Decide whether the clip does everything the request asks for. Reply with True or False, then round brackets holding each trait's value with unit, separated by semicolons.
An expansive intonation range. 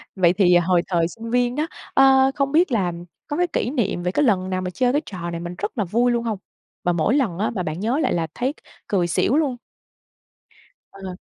True (6.5 semitones)